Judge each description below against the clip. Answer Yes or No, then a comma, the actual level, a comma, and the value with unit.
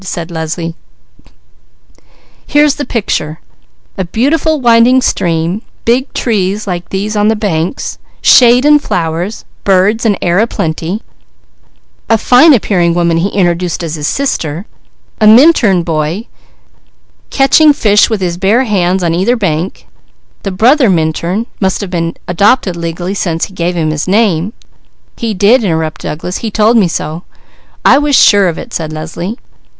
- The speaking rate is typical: Yes, average, 150 wpm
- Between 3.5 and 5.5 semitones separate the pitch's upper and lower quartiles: Yes, average, 5.1 semitones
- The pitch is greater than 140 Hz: Yes, high, 190 Hz